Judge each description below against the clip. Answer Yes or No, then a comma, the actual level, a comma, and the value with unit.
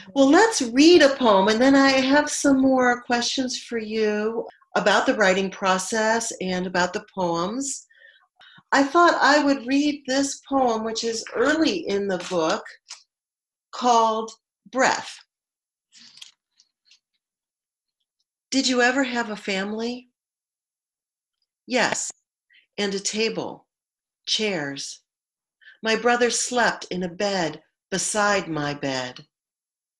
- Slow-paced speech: Yes, slow, 115 wpm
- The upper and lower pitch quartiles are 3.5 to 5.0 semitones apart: No, wide, 5.4 semitones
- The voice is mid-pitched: No, high, 225 Hz